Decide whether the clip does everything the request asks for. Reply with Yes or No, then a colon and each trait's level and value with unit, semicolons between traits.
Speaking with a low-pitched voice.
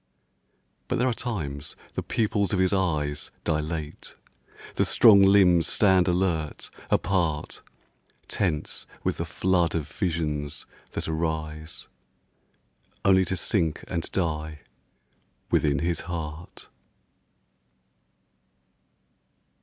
Yes: very low, 85 Hz